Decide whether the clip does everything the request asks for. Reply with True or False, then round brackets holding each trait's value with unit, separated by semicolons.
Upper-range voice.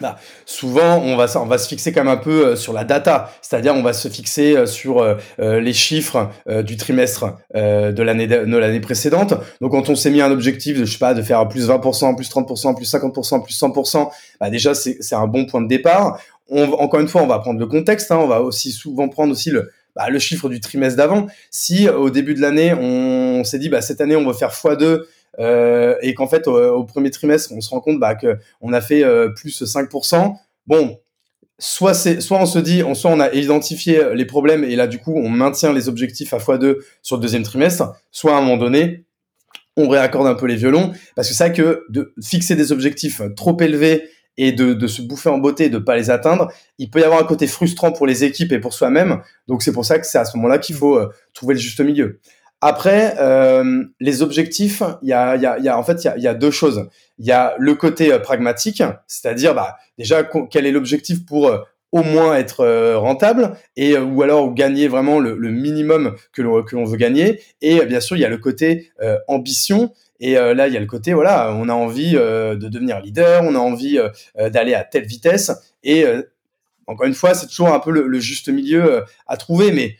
False (140 Hz)